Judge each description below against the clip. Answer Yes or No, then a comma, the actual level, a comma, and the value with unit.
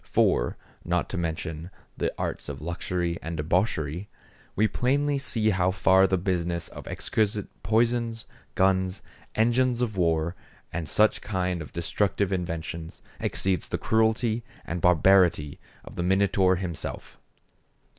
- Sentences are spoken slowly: Yes, slow, 130 wpm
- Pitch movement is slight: No, average, 4.0 semitones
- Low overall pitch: Yes, very low, 95 Hz